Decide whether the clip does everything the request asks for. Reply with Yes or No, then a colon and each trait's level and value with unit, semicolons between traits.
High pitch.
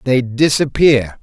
No: low, 130 Hz